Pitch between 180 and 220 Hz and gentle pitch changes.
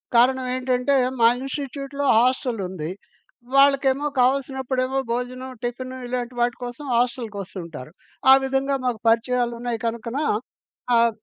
No: very high, 250 Hz; narrow, 2.2 semitones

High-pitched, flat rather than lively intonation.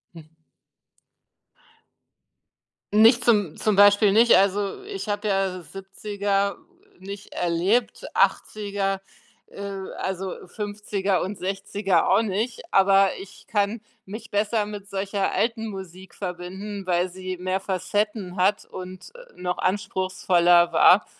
Yes: high, 195 Hz; narrow, 1.8 semitones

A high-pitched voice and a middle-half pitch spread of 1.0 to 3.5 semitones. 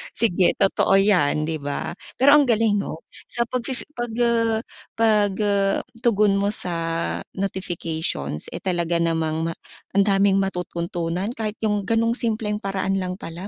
No: high, 195 Hz; average, 4.2 semitones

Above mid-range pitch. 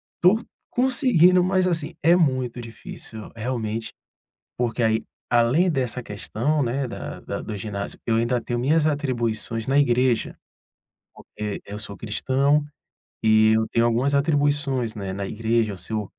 No: low, 120 Hz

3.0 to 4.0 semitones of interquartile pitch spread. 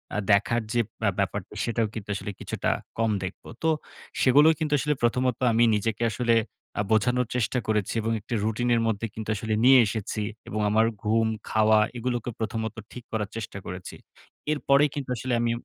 No: narrow, 2.4 semitones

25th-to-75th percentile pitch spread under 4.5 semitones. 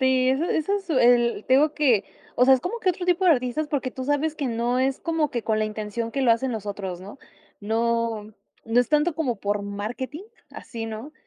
No: average, 4.9 semitones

